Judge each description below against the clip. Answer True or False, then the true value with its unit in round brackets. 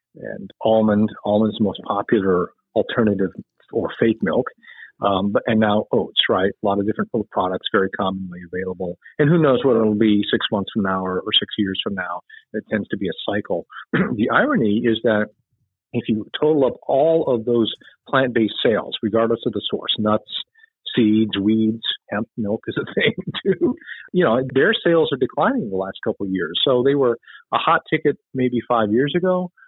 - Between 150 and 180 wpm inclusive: False (190 wpm)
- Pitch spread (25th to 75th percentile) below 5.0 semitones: True (4.5 semitones)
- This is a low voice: True (110 Hz)